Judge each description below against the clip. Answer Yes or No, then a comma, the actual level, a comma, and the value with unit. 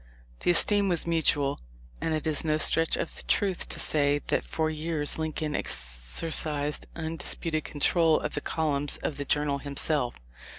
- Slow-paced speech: No, average, 160 wpm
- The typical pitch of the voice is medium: Yes, medium, 155 Hz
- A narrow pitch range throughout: Yes, narrow, 2.1 semitones